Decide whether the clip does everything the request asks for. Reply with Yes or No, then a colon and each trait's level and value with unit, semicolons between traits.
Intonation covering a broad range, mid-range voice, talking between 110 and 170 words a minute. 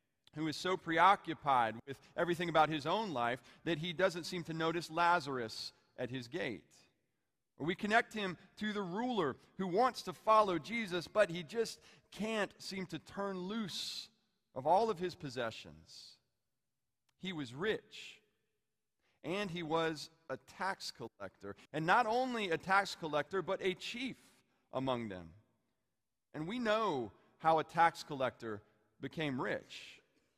Yes: wide, 6.6 semitones; medium, 165 Hz; average, 145 wpm